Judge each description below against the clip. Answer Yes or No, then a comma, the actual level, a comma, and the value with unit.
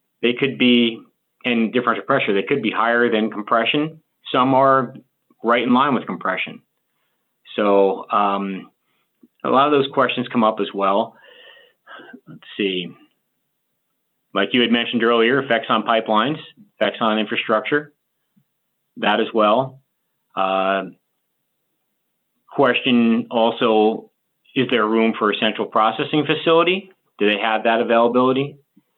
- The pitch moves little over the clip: No, average, 3.8 semitones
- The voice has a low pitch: Yes, low, 115 Hz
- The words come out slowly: Yes, slow, 130 wpm